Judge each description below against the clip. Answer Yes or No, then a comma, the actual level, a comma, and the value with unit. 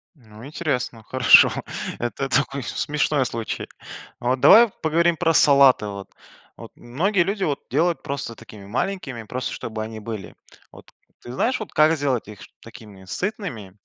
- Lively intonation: Yes, wide, 6.1 semitones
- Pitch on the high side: No, low, 130 Hz